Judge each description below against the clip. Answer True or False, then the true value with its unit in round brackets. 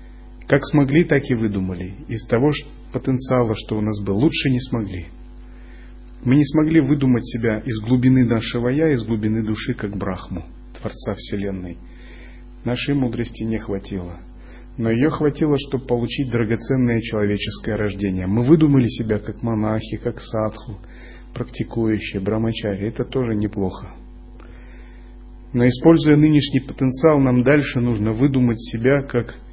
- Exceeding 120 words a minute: True (130 wpm)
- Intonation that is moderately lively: True (3.9 semitones)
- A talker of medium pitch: False (115 Hz)